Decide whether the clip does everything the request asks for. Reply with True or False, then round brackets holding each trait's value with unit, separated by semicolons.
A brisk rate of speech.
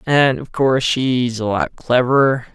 False (165 wpm)